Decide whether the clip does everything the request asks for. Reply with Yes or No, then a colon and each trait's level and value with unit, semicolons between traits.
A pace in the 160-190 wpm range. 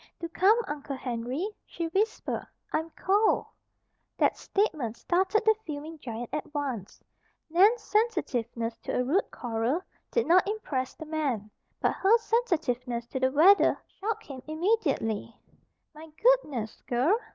No: slow, 135 wpm